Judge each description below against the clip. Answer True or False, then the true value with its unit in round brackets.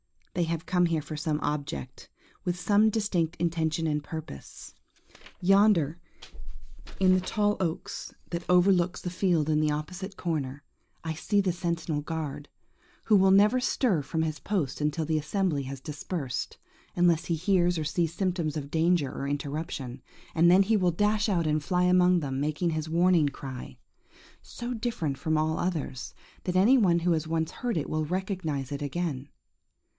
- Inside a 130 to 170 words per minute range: True (165 wpm)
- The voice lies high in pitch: False (165 Hz)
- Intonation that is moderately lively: True (3.4 semitones)